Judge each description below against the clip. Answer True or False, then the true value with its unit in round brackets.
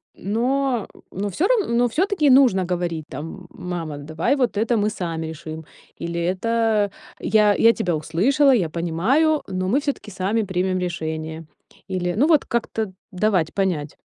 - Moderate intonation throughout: False (5.7 semitones)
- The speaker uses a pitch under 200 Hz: True (190 Hz)